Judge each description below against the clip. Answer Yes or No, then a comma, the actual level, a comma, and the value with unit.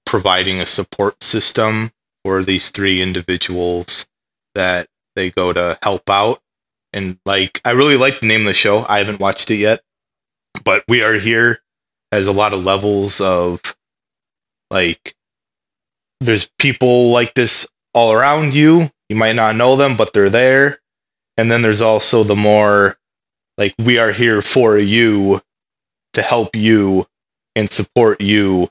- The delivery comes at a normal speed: Yes, average, 155 wpm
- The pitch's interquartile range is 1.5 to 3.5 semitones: Yes, average, 3.2 semitones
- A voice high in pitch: No, low, 105 Hz